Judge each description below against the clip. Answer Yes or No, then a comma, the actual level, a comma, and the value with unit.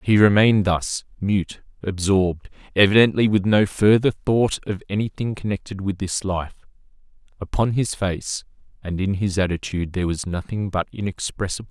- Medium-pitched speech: No, low, 100 Hz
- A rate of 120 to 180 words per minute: Yes, average, 150 wpm